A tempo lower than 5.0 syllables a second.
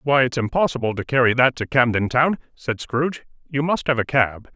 No: 5.4 syllables/s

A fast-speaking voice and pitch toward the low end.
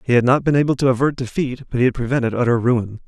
Yes: fast, 275 wpm; low, 125 Hz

